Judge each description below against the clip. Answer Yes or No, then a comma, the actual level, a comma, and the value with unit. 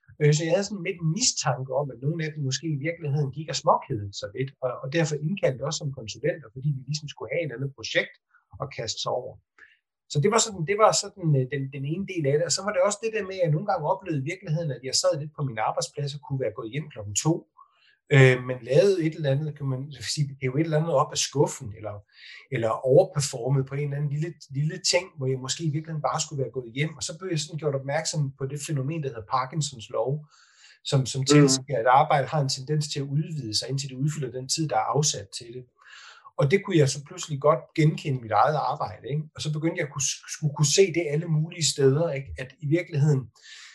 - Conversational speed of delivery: No, fast, 245 wpm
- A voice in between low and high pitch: Yes, medium, 150 Hz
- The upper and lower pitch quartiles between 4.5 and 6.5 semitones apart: No, average, 3.2 semitones